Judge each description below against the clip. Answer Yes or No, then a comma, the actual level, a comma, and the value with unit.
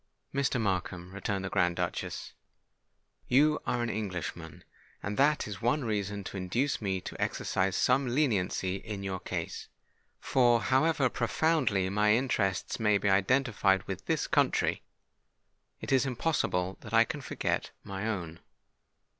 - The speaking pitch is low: Yes, low, 105 Hz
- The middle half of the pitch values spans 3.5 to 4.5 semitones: No, average, 5.1 semitones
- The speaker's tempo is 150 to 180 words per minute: No, average, 140 wpm